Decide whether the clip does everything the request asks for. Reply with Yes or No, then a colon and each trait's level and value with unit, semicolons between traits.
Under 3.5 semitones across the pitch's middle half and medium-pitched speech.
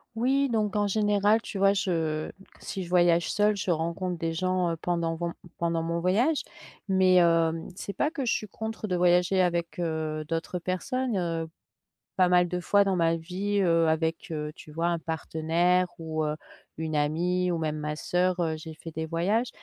Yes: average, 3.0 semitones; medium, 175 Hz